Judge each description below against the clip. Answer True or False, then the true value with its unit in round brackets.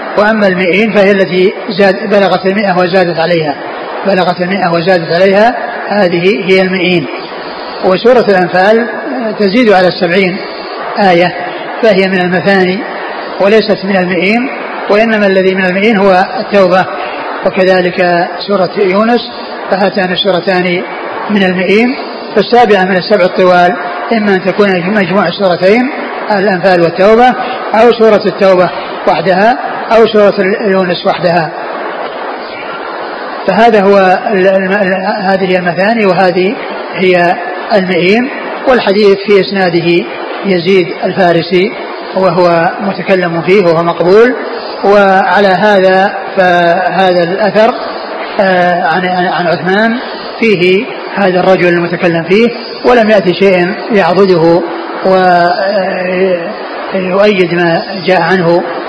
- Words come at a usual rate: True (100 wpm)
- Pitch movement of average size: False (2.1 semitones)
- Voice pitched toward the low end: False (190 Hz)